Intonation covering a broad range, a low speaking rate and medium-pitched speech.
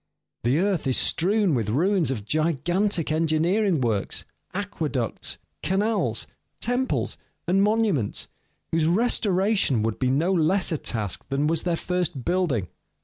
Yes: wide, 6.3 semitones; slow, 130 wpm; medium, 165 Hz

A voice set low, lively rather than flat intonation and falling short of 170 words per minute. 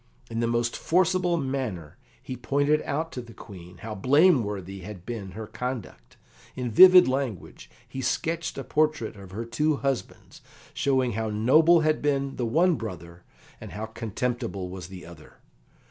Yes: low, 120 Hz; wide, 5.8 semitones; average, 160 wpm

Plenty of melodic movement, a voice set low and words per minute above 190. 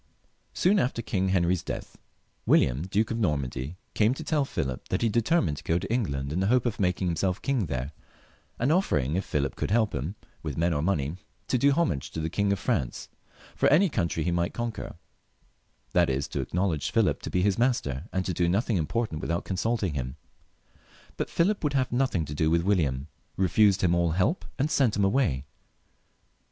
Yes: wide, 7.0 semitones; very low, 95 Hz; average, 200 wpm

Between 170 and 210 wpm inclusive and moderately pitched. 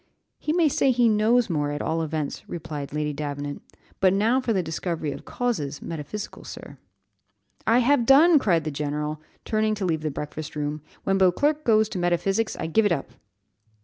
Yes: average, 180 wpm; medium, 175 Hz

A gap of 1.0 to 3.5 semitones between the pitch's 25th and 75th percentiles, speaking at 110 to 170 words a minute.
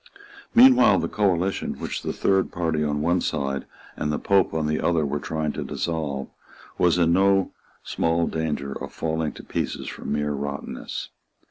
Yes: average, 3.2 semitones; average, 165 wpm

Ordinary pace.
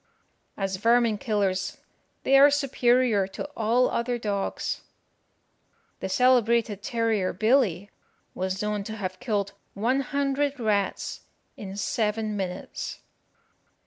No: slow, 110 wpm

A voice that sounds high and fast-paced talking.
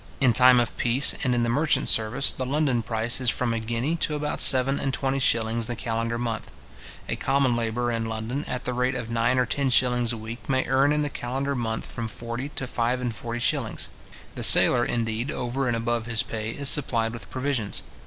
No: low, 120 Hz; fast, 215 wpm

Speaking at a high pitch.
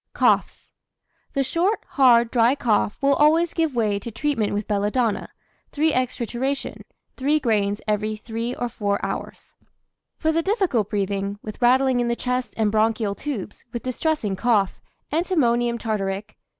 Yes: high, 235 Hz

